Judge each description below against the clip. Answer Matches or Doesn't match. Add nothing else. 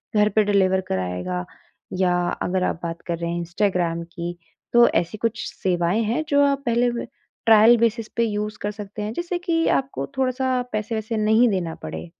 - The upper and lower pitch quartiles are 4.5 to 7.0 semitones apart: Matches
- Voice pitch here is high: Matches